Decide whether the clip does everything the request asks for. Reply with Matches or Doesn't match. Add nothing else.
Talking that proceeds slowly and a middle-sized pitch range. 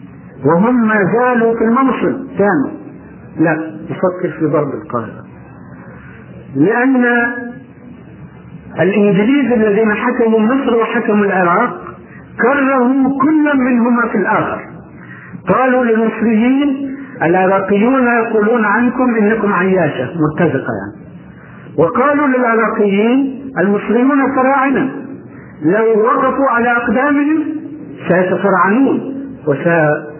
Doesn't match